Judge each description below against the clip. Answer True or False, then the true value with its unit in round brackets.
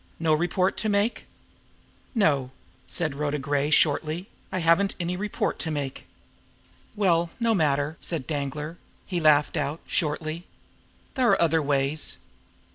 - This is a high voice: False (160 Hz)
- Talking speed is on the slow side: True (130 wpm)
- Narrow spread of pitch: False (3.4 semitones)